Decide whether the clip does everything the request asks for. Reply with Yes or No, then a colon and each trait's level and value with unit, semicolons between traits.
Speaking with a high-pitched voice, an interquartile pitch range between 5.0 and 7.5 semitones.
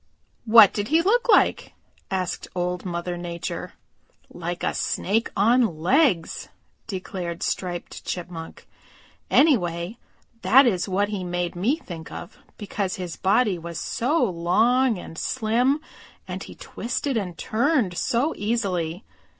Yes: high, 195 Hz; wide, 5.4 semitones